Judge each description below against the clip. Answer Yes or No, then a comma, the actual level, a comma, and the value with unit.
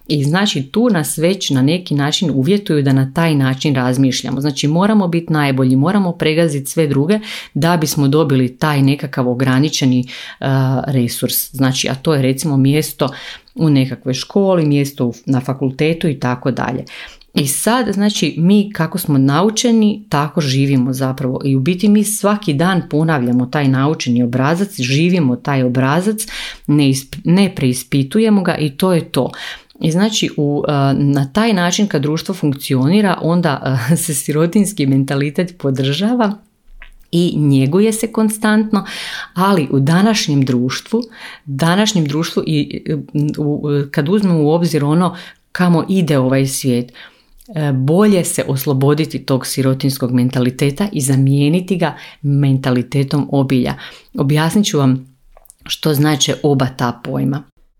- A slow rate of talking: No, average, 135 wpm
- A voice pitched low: No, medium, 150 Hz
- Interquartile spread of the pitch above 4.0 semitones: Yes, average, 4.6 semitones